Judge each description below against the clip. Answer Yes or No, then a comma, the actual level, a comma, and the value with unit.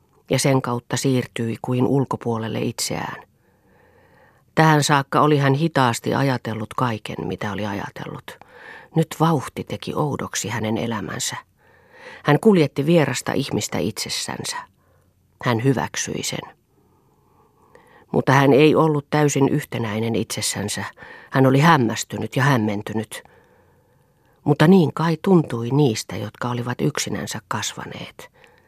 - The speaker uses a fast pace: No, average, 110 wpm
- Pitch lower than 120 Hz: No, low, 130 Hz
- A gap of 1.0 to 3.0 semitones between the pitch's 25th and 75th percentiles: No, average, 4.8 semitones